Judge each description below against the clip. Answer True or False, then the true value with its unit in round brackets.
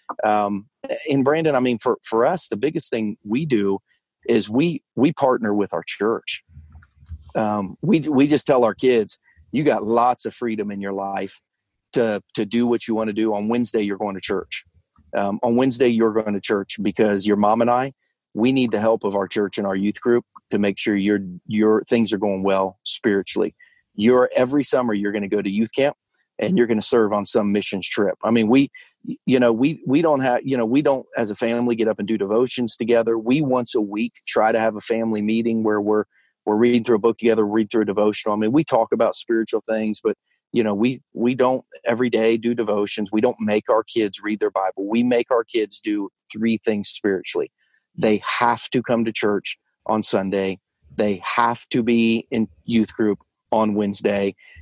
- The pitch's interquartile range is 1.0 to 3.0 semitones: True (2.6 semitones)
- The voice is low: True (110 Hz)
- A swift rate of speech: True (215 wpm)